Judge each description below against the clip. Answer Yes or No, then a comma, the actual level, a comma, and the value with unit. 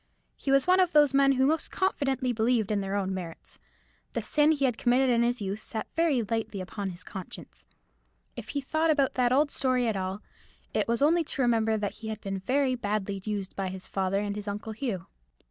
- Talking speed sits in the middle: No, fast, 215 wpm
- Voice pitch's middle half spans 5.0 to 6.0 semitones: Yes, average, 5.3 semitones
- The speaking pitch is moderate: No, high, 230 Hz